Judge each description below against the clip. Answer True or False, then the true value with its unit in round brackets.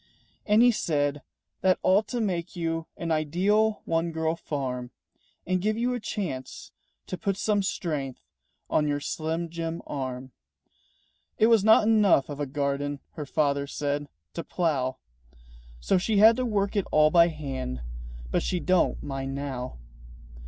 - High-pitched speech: False (165 Hz)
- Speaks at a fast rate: False (155 wpm)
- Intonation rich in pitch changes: True (5.7 semitones)